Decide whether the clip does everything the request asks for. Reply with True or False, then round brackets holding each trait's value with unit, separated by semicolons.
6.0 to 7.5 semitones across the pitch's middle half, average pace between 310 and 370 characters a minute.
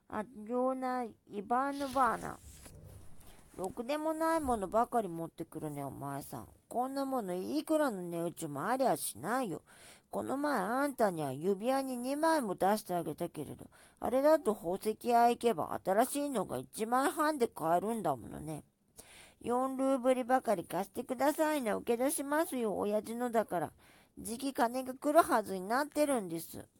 True (7.0 semitones; 325 characters per minute)